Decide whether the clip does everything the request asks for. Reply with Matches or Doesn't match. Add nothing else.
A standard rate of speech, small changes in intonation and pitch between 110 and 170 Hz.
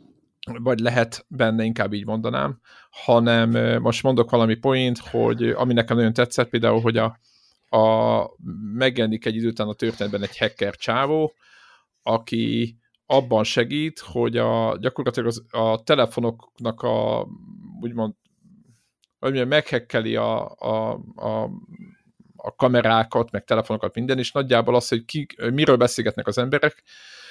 Matches